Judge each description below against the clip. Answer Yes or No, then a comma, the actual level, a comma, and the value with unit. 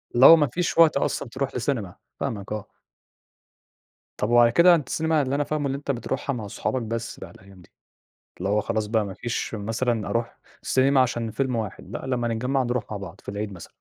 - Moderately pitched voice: No, low, 120 Hz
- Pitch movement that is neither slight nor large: Yes, average, 4.2 semitones